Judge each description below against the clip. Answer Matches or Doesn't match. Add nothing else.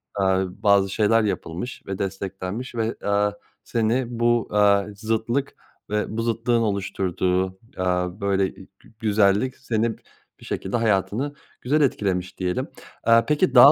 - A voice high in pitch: Doesn't match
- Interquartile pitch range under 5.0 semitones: Matches